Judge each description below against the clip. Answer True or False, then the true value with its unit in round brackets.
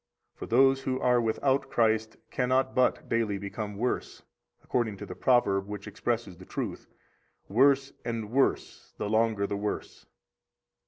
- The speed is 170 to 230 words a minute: False (150 wpm)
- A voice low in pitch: True (115 Hz)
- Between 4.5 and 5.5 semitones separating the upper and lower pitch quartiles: False (3.6 semitones)